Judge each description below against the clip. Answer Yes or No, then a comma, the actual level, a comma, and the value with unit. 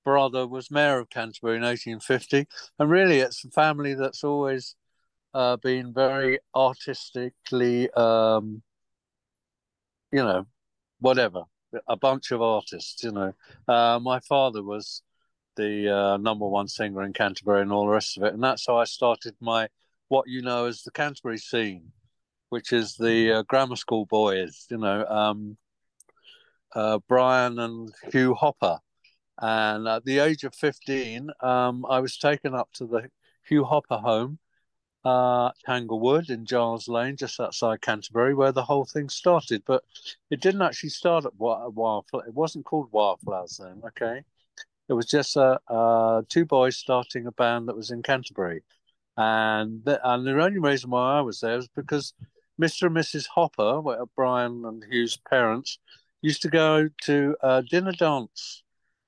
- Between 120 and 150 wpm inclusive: No, average, 160 wpm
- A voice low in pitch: Yes, low, 125 Hz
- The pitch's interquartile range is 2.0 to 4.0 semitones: Yes, average, 3.5 semitones